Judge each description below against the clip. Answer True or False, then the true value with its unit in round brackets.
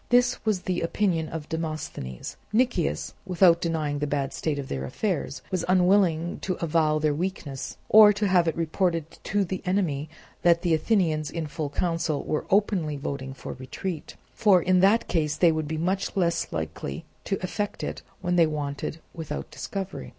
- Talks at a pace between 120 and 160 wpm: False (170 wpm)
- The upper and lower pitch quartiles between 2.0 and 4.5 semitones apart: True (3.6 semitones)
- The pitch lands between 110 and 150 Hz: False (165 Hz)